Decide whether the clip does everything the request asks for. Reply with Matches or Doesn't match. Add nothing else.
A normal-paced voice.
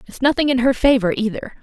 Doesn't match